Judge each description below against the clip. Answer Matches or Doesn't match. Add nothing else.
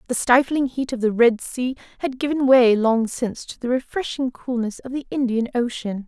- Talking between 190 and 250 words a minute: Matches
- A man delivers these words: Doesn't match